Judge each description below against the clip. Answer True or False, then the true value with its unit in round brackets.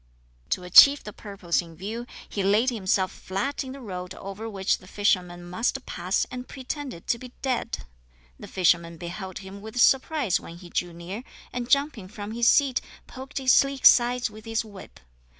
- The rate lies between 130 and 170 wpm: False (180 wpm)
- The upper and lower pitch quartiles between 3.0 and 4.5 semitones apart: False (5.2 semitones)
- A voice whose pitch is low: False (210 Hz)